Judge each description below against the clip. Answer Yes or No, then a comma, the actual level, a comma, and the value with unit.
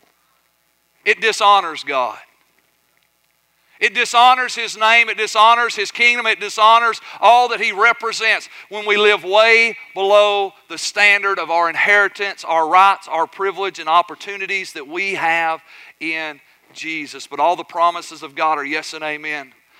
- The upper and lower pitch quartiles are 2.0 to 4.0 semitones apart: No, average, 5.0 semitones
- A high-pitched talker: Yes, high, 200 Hz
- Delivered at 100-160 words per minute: Yes, average, 145 wpm